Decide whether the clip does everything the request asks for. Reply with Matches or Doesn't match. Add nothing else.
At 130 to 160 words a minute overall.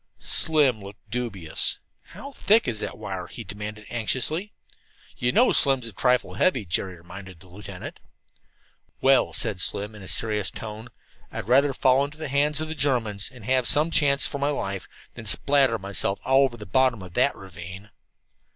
Doesn't match